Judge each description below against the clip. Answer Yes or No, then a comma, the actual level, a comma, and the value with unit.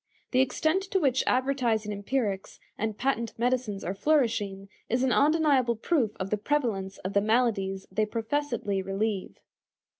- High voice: Yes, high, 230 Hz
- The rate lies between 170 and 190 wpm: No, average, 145 wpm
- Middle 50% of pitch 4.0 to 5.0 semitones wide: Yes, average, 4.7 semitones